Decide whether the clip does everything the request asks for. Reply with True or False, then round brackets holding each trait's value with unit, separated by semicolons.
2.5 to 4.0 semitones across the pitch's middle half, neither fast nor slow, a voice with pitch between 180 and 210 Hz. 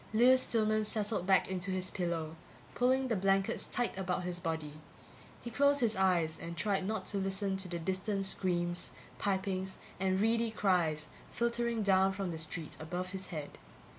True (3.3 semitones; 165 wpm; 190 Hz)